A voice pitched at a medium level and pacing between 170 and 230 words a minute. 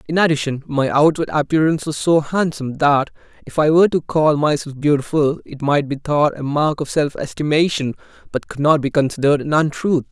Yes: medium, 150 Hz; average, 190 wpm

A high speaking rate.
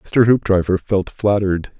No: slow, 135 wpm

